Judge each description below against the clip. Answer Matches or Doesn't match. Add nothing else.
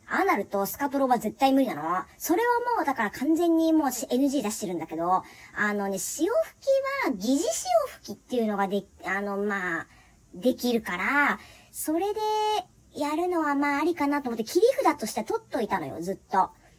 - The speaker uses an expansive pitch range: Matches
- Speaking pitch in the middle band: Doesn't match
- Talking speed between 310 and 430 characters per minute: Matches